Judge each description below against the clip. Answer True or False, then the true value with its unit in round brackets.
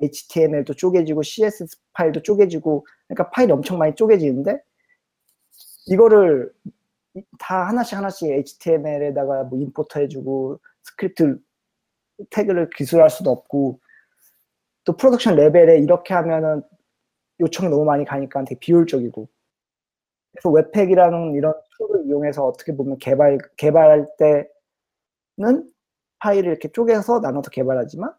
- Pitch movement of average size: False (5.8 semitones)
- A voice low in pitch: False (160 Hz)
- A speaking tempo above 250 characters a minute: True (320 characters per minute)